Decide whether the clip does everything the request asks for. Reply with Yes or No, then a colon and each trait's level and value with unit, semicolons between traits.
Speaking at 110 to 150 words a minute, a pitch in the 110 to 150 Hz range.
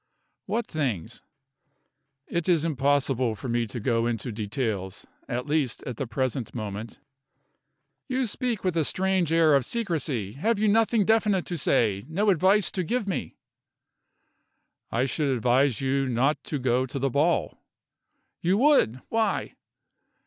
Yes: average, 145 wpm; medium, 140 Hz